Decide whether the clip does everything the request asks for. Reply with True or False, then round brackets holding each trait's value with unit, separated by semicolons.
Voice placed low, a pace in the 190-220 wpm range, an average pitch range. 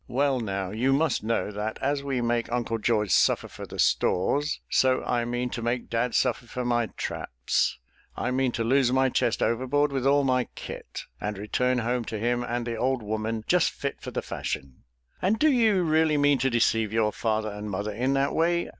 True (120 Hz; 205 wpm; 3.4 semitones)